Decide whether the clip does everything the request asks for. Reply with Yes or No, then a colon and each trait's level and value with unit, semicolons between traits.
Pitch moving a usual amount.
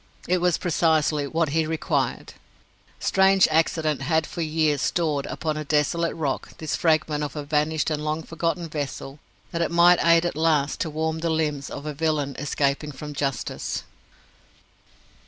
No: narrow, 1.9 semitones